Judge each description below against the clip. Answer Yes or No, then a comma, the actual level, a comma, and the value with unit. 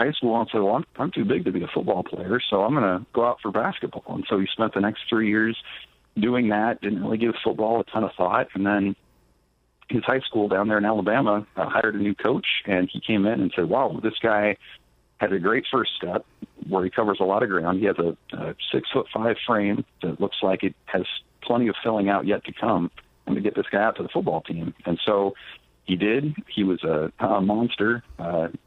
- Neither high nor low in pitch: No, low, 105 Hz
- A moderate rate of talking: No, fast, 240 wpm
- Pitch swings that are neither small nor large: Yes, average, 3.4 semitones